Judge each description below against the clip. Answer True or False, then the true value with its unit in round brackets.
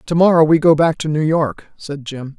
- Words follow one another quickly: True (250 wpm)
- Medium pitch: True (155 Hz)